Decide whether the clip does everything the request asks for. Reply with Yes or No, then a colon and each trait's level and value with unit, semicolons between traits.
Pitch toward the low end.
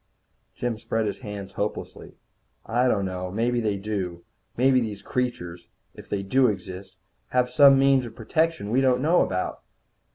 Yes: low, 115 Hz